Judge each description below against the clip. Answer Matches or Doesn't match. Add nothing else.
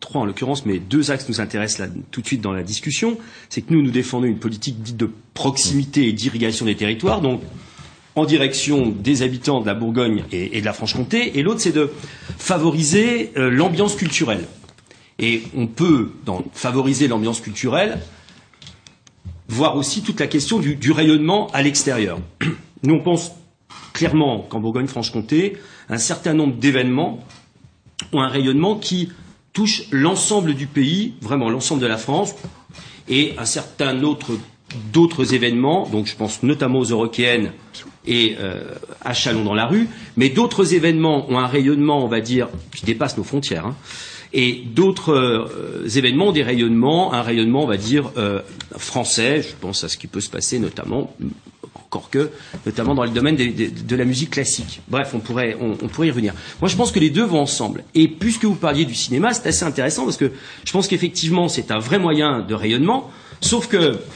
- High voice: Doesn't match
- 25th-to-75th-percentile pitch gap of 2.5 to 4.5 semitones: Doesn't match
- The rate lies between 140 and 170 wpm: Doesn't match